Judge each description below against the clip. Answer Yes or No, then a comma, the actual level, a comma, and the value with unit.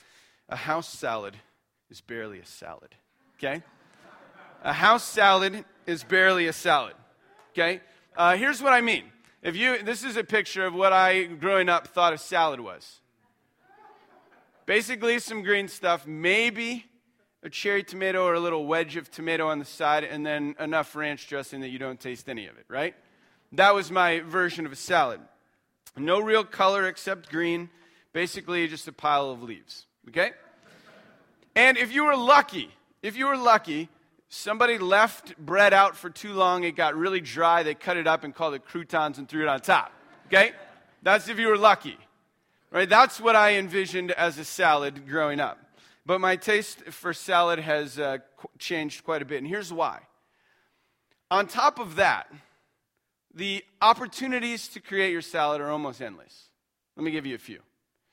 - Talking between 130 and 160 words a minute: No, average, 175 wpm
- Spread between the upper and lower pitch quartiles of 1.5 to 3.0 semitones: No, average, 4.9 semitones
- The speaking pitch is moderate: Yes, medium, 180 Hz